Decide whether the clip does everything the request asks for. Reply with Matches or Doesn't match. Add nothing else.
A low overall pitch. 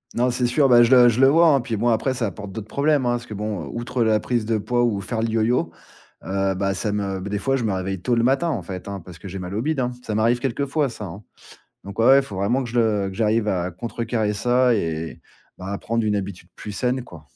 Matches